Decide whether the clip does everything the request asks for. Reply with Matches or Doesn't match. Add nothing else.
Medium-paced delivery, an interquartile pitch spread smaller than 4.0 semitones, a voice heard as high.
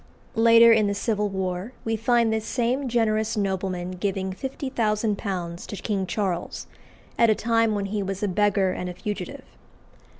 Matches